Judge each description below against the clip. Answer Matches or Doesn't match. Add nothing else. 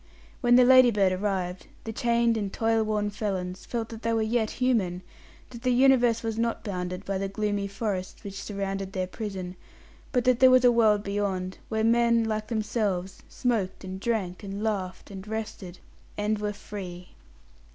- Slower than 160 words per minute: Doesn't match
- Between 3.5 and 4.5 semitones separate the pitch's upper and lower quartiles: Doesn't match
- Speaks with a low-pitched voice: Doesn't match